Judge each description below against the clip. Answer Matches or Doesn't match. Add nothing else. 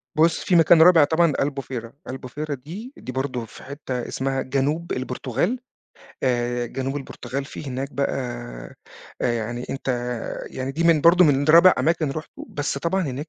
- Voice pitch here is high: Doesn't match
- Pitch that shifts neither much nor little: Matches